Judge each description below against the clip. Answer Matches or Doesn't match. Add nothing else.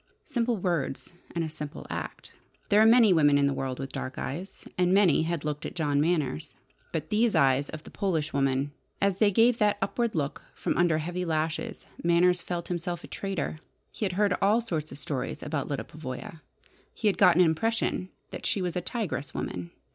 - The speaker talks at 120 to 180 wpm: Doesn't match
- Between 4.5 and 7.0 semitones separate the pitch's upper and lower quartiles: Matches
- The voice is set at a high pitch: Doesn't match